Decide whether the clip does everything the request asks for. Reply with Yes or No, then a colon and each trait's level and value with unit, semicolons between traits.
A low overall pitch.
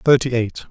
Yes: low, 120 Hz